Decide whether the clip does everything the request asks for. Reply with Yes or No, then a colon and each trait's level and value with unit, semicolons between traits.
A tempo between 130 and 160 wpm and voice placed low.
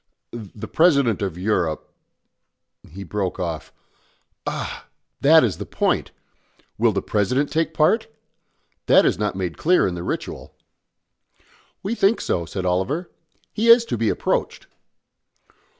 Yes: slow, 135 wpm; low, 110 Hz